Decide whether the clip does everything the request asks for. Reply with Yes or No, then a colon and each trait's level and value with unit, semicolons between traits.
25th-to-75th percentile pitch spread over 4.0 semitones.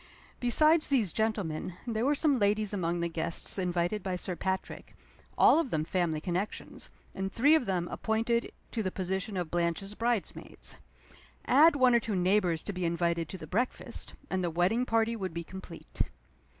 Yes: average, 4.7 semitones